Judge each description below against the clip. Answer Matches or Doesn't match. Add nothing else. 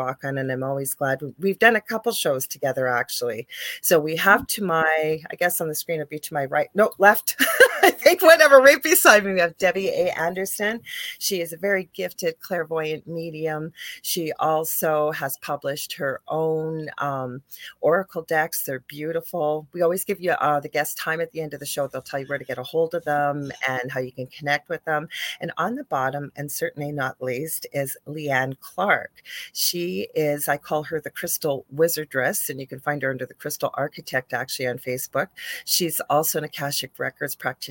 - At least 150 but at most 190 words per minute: Doesn't match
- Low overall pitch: Doesn't match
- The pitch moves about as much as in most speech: Matches